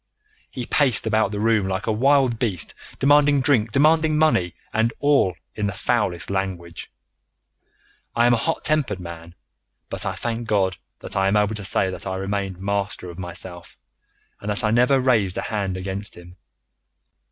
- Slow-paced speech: No, average, 175 wpm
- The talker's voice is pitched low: Yes, low, 105 Hz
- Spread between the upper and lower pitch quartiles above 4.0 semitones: Yes, average, 4.5 semitones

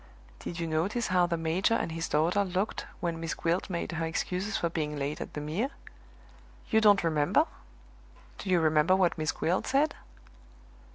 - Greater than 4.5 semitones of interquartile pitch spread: No, average, 3.0 semitones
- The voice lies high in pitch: No, medium, 170 Hz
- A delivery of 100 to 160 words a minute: No, average, 175 wpm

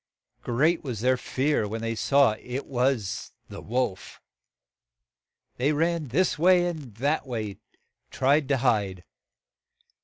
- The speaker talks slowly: Yes, slow, 130 wpm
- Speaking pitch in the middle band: No, low, 130 Hz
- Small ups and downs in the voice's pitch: No, average, 4.5 semitones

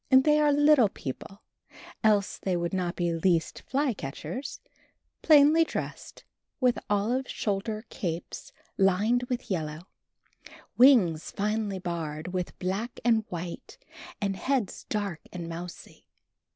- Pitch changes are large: Yes, wide, 6.0 semitones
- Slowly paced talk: Yes, slow, 120 wpm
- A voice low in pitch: No, high, 200 Hz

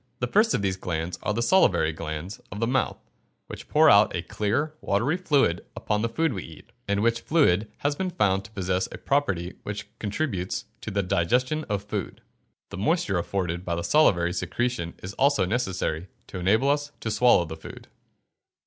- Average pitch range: No, wide, 6.4 semitones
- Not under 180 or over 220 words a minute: Yes, average, 185 wpm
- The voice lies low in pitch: Yes, low, 105 Hz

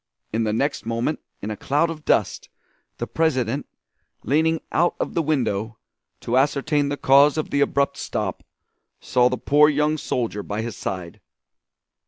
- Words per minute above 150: Yes, average, 160 wpm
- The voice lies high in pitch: No, medium, 140 Hz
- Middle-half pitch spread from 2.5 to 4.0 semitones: No, average, 4.6 semitones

